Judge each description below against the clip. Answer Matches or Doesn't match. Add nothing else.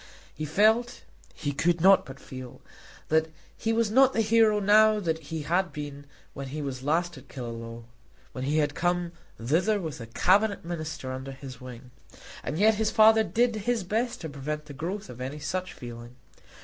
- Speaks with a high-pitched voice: Doesn't match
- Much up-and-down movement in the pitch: Matches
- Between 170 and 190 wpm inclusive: Matches